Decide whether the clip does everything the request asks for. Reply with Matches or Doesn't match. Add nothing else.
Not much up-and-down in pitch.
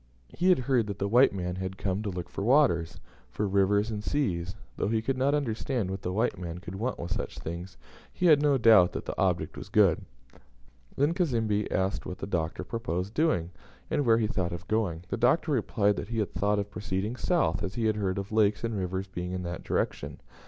Doesn't match